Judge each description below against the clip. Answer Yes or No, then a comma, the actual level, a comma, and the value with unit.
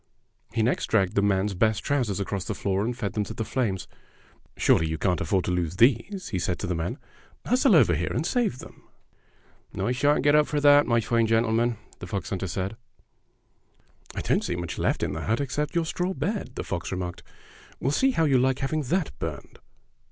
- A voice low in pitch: Yes, low, 115 Hz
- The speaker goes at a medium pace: No, fast, 210 wpm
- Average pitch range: No, wide, 7.2 semitones